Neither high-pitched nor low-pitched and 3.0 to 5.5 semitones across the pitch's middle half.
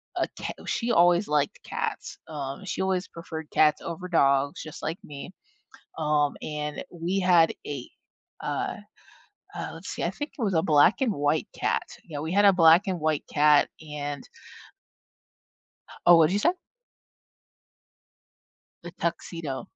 Yes: medium, 160 Hz; average, 3.4 semitones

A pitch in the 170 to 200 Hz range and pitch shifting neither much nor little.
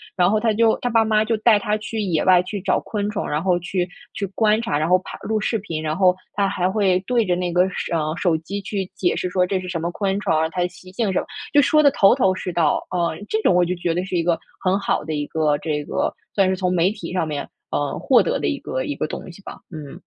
Yes: medium, 185 Hz; average, 3.5 semitones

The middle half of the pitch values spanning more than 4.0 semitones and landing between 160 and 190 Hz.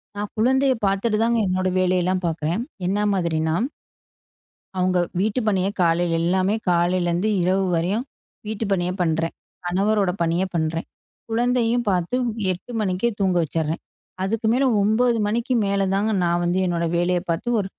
No: average, 3.7 semitones; medium, 185 Hz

